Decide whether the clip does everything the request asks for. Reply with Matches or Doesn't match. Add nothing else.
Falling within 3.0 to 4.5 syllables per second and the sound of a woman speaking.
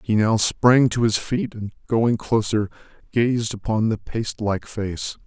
Doesn't match